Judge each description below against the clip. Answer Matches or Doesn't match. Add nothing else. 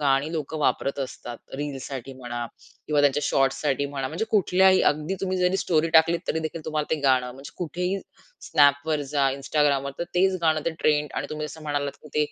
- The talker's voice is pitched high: Doesn't match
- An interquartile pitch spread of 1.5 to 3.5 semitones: Matches